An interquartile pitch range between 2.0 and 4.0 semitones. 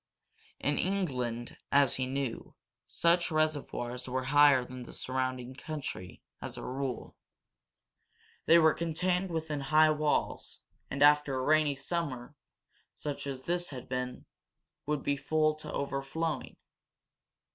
Yes: average, 3.2 semitones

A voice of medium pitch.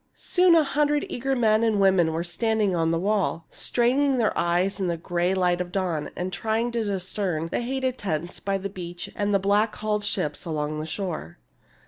No: high, 195 Hz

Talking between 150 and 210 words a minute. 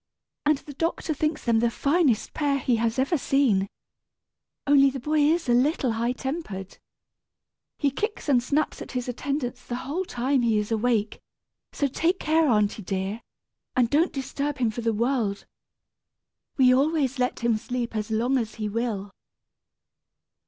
Yes: average, 160 wpm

